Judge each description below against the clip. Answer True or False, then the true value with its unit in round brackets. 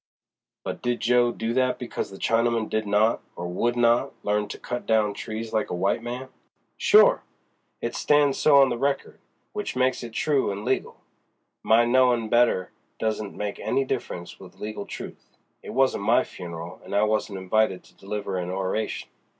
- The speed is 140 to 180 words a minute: True (175 wpm)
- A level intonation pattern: False (3.2 semitones)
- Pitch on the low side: True (110 Hz)